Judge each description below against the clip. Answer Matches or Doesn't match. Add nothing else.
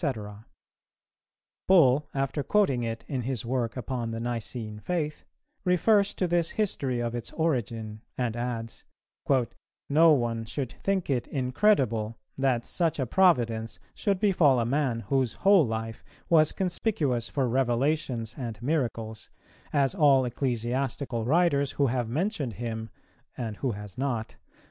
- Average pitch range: Matches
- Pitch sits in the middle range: Doesn't match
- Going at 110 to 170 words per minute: Matches